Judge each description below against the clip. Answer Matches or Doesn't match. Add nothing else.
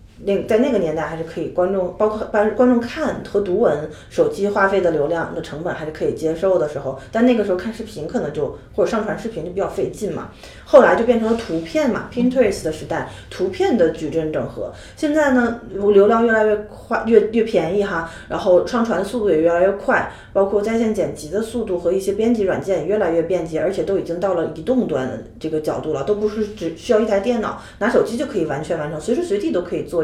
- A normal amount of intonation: Matches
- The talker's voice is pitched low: Doesn't match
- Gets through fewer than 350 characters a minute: Doesn't match